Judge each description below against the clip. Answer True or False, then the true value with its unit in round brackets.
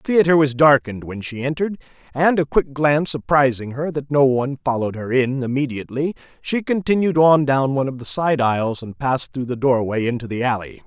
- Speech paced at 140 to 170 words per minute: False (205 wpm)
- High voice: False (135 Hz)